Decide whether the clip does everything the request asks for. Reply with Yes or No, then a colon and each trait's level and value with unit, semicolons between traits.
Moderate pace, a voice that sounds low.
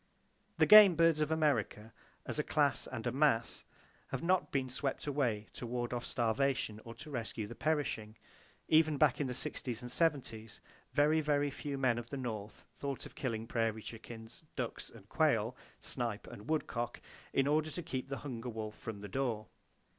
Yes: average, 180 wpm; low, 125 Hz